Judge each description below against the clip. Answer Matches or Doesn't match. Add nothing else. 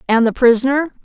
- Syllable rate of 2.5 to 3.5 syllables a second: Doesn't match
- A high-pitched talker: Matches